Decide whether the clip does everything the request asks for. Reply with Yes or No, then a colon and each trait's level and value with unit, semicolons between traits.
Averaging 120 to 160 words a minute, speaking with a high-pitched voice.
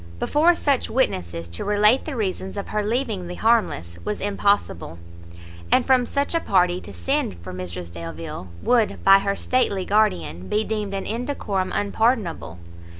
Yes: average, 155 wpm; high, 200 Hz